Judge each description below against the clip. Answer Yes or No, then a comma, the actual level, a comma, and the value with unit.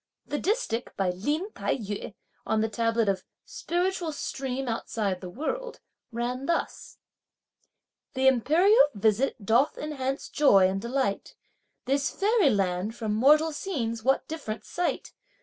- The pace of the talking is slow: Yes, slow, 130 wpm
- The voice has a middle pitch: No, very high, 255 Hz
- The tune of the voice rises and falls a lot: Yes, wide, 5.9 semitones